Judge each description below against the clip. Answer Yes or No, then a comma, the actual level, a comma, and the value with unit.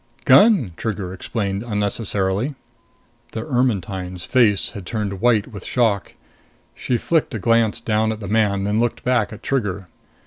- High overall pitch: No, low, 110 Hz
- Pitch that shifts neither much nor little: Yes, average, 3.1 semitones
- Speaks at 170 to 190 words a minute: No, average, 145 wpm